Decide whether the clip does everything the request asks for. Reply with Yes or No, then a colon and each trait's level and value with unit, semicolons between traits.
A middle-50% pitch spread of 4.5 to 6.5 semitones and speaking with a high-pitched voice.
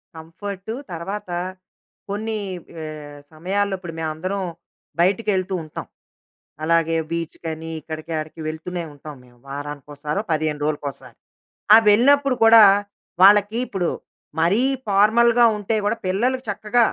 No: average, 4.9 semitones; medium, 180 Hz